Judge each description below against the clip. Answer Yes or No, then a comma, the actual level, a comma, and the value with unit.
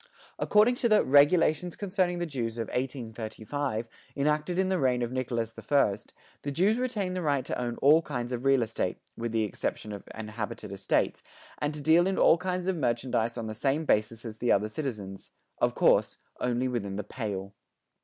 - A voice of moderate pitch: No, low, 130 Hz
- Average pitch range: No, wide, 6.1 semitones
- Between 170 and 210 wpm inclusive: Yes, average, 190 wpm